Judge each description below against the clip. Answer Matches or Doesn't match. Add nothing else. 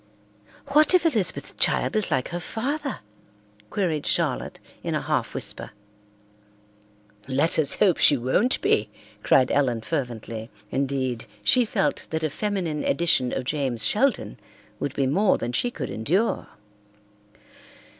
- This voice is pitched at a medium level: Matches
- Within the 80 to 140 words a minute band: Matches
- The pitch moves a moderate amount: Doesn't match